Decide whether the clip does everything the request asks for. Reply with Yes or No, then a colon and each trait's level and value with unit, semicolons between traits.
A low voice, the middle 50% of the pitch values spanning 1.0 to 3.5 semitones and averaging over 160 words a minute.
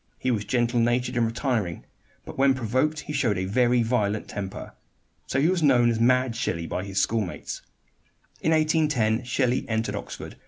Yes: low, 120 Hz; average, 2.8 semitones; average, 170 wpm